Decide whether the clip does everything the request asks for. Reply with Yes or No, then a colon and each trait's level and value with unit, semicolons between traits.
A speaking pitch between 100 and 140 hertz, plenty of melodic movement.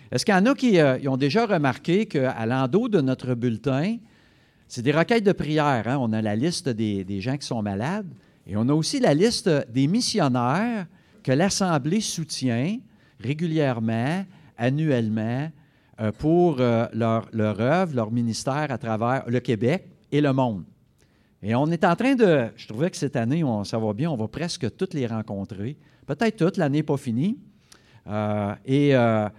Yes: low, 135 Hz; wide, 6.6 semitones